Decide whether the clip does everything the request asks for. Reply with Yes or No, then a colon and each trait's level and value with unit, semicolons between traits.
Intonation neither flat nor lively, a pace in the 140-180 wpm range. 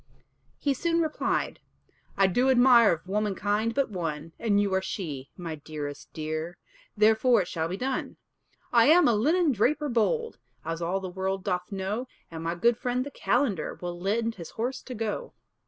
No: wide, 6.0 semitones; average, 175 wpm